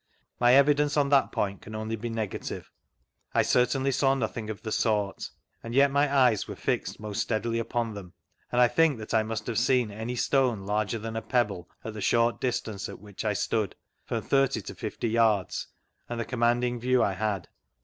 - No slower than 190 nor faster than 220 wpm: Yes, average, 200 wpm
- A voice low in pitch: Yes, low, 115 Hz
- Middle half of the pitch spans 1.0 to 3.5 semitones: Yes, average, 2.7 semitones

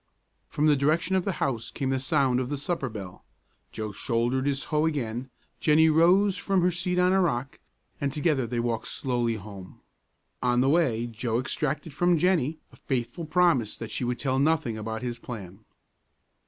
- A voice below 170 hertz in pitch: Yes, low, 135 Hz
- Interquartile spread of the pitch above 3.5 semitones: Yes, average, 5.2 semitones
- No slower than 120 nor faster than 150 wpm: No, average, 180 wpm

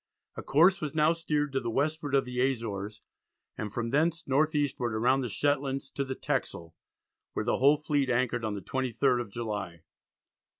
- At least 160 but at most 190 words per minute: Yes, average, 180 wpm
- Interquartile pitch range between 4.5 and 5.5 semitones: No, average, 4.0 semitones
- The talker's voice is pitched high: No, low, 130 Hz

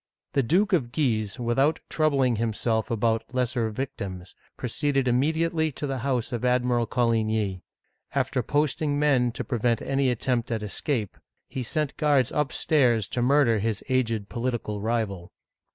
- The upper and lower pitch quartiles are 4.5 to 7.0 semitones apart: No, average, 3.6 semitones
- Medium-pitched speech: No, low, 125 Hz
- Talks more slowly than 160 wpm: Yes, average, 145 wpm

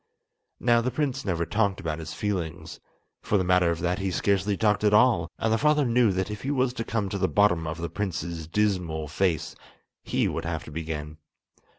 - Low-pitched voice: Yes, very low, 95 Hz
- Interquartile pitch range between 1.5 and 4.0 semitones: No, average, 4.5 semitones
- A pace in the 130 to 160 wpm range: No, fast, 205 wpm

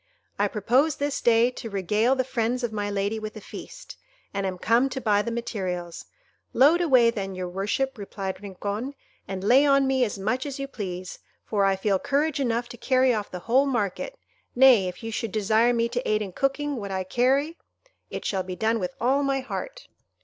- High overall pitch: Yes, high, 230 Hz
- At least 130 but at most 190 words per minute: No, fast, 205 wpm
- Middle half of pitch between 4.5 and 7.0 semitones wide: Yes, average, 4.9 semitones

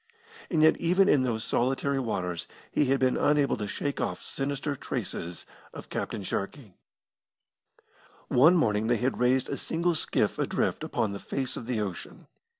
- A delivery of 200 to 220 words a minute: No, average, 160 wpm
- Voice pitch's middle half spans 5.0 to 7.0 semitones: No, average, 4.6 semitones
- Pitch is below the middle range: Yes, low, 130 Hz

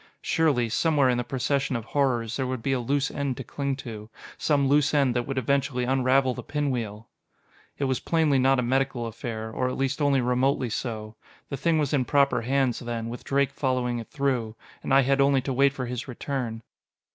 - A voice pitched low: Yes, low, 130 Hz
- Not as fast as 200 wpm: No, fast, 205 wpm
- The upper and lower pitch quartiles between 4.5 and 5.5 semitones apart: No, narrow, 2.4 semitones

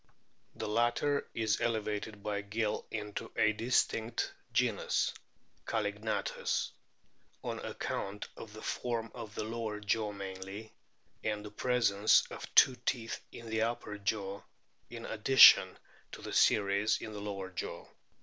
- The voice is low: Yes, low, 105 Hz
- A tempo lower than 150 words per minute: Yes, slow, 135 wpm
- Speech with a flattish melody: Yes, narrow, 1.8 semitones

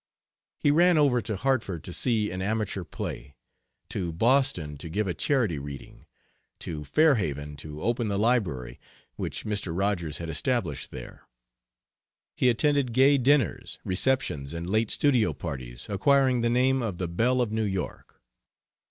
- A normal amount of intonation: No, wide, 7.4 semitones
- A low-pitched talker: Yes, low, 105 Hz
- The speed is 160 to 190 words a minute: No, average, 150 wpm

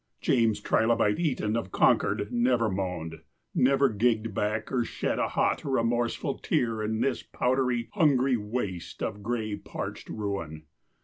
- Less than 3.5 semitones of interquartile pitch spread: Yes, average, 3.0 semitones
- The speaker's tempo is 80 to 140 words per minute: Yes, slow, 135 wpm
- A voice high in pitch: No, low, 115 Hz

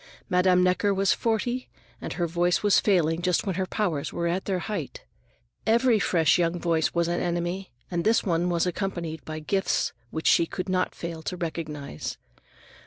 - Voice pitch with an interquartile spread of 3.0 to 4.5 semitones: No, narrow, 2.5 semitones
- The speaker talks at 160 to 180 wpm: Yes, average, 175 wpm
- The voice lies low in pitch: No, medium, 175 Hz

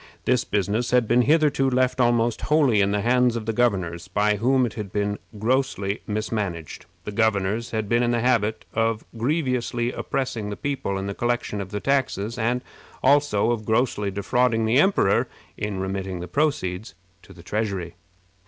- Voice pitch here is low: Yes, low, 115 Hz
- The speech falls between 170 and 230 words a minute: Yes, average, 175 wpm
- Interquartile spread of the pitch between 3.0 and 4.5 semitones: Yes, average, 3.7 semitones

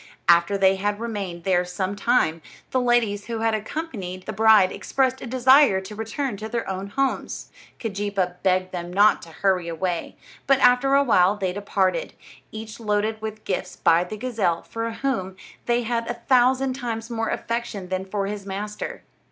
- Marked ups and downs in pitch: No, average, 4.0 semitones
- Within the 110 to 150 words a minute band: No, average, 175 wpm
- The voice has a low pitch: No, high, 210 Hz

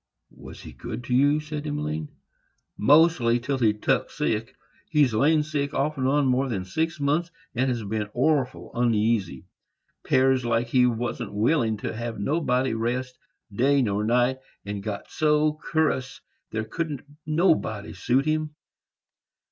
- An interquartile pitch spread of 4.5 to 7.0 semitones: Yes, average, 4.8 semitones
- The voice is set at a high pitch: No, low, 125 Hz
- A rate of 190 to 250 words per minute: No, average, 145 wpm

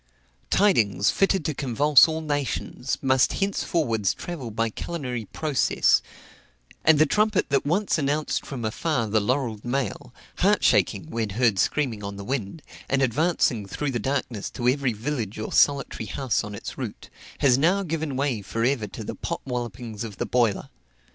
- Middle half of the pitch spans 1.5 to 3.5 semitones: No, average, 5.0 semitones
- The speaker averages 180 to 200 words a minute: No, average, 165 wpm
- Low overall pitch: Yes, low, 130 Hz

